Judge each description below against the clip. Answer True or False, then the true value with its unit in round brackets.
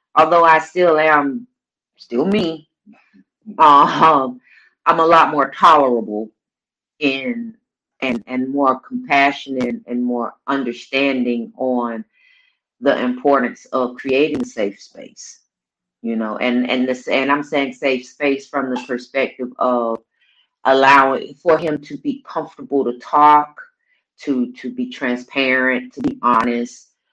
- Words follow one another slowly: True (125 wpm)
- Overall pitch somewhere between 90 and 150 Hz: True (135 Hz)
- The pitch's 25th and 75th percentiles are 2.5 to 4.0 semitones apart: False (4.4 semitones)